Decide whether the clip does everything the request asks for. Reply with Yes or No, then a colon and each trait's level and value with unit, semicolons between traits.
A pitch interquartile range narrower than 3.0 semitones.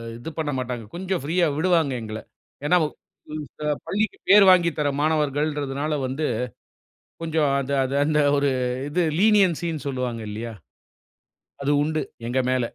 No: average, 4.0 semitones